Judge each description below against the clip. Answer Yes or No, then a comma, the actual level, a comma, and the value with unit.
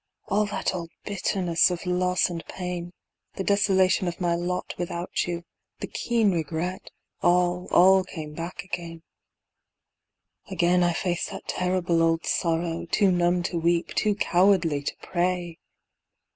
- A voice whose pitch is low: No, medium, 175 Hz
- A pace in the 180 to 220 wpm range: No, average, 140 wpm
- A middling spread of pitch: No, narrow, 1.5 semitones